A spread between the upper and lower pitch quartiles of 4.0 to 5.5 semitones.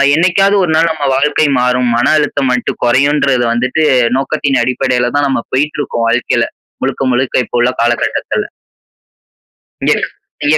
No: average, 3.2 semitones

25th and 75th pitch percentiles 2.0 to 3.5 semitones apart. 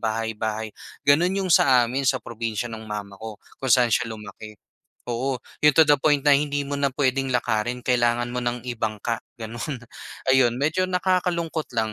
No: average, 4.2 semitones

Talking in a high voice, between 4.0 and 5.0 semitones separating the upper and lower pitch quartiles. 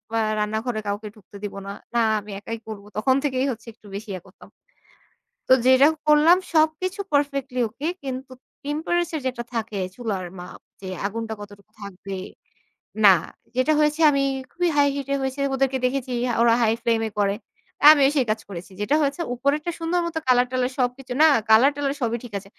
Yes: very high, 255 Hz; average, 4.7 semitones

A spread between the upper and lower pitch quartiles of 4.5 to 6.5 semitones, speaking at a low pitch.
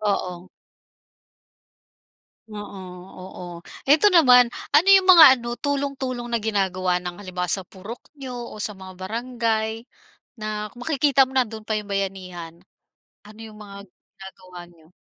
No: average, 4.9 semitones; high, 215 Hz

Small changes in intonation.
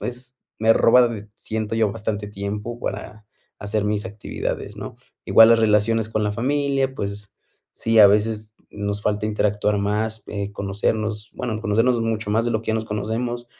Yes: narrow, 1.5 semitones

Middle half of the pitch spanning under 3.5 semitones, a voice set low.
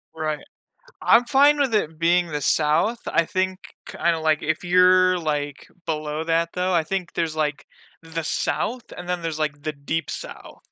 No: average, 2.9 semitones; medium, 165 Hz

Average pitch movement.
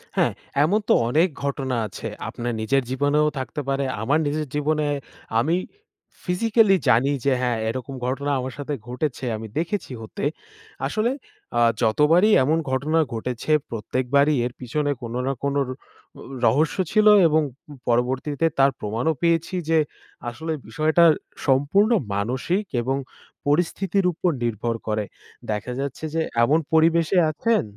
Yes: average, 4.4 semitones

